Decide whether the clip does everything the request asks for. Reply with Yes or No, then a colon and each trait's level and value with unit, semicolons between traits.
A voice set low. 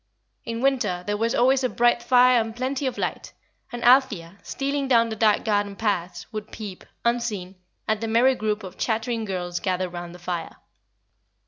No: high, 220 Hz